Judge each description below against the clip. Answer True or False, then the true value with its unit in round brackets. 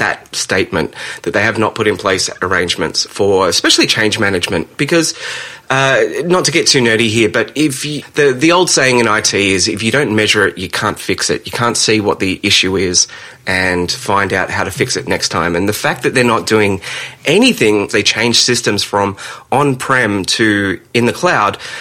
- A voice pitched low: True (115 Hz)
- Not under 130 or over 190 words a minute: False (205 wpm)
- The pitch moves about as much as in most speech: False (6.4 semitones)